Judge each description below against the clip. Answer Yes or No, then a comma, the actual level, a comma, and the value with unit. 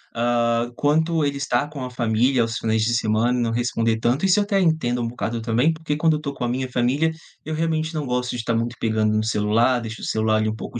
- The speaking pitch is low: Yes, low, 120 Hz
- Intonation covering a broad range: No, average, 4.4 semitones